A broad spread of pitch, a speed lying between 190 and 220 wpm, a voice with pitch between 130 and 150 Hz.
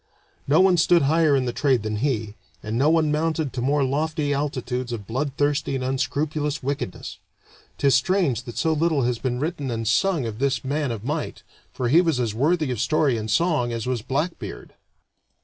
No: average, 4.0 semitones; average, 195 wpm; medium, 140 Hz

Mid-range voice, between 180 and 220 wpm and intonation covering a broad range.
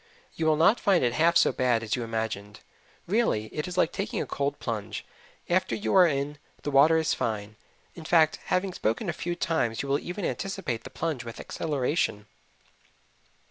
Yes: medium, 150 Hz; average, 185 wpm; wide, 6.8 semitones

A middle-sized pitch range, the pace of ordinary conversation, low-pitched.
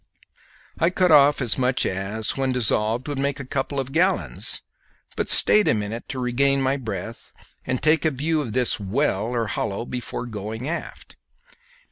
Yes: average, 4.1 semitones; average, 170 wpm; low, 130 Hz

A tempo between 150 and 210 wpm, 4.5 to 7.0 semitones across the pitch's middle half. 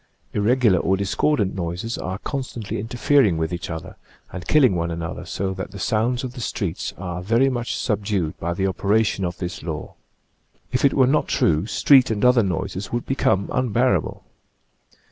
Yes: average, 170 wpm; wide, 5.4 semitones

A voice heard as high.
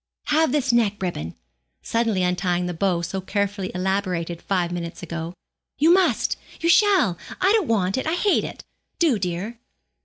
Yes: high, 195 Hz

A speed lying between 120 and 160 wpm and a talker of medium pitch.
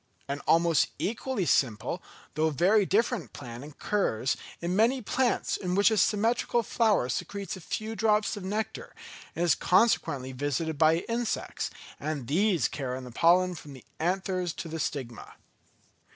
Yes: average, 150 wpm; medium, 180 Hz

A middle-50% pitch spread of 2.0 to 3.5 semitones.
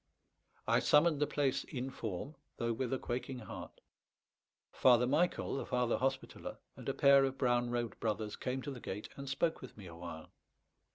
Yes: narrow, 2.6 semitones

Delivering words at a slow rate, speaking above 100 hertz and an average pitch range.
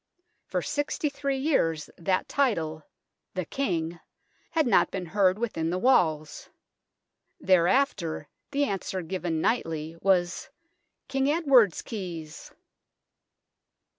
No: slow, 105 wpm; medium, 185 Hz; wide, 8.4 semitones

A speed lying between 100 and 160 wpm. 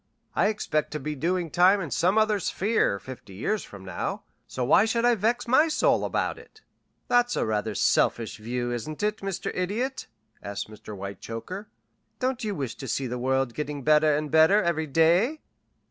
No: average, 180 wpm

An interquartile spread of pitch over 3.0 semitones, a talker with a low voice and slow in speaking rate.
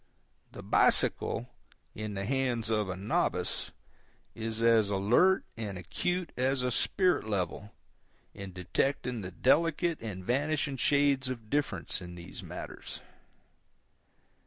Yes: wide, 5.6 semitones; low, 115 Hz; slow, 125 wpm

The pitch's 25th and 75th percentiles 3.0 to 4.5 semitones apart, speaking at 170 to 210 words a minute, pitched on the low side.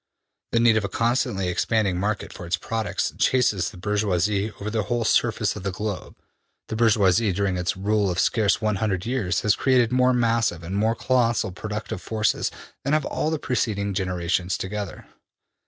Yes: average, 3.3 semitones; average, 175 wpm; low, 105 Hz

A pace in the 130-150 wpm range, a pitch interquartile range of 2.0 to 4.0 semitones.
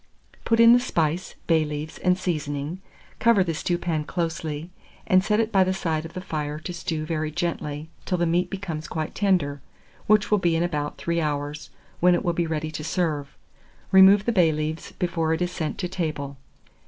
No: average, 195 wpm; average, 3.1 semitones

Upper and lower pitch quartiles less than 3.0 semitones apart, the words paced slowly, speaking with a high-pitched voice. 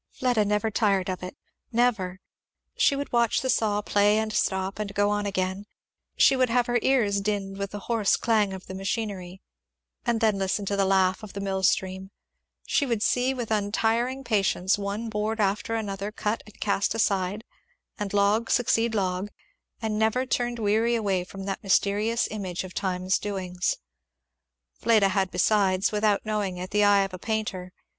No: narrow, 2.5 semitones; average, 180 wpm; high, 205 Hz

